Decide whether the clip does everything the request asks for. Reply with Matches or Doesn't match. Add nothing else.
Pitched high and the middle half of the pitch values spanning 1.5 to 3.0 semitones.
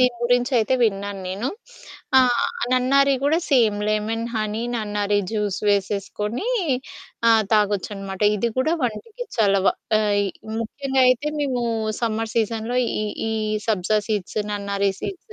Doesn't match